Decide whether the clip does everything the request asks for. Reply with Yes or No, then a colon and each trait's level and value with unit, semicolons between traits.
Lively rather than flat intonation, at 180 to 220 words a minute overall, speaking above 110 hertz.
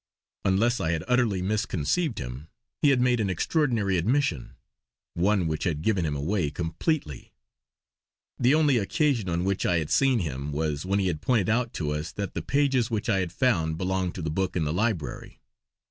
No: wide, 6.7 semitones; average, 190 wpm; very low, 95 Hz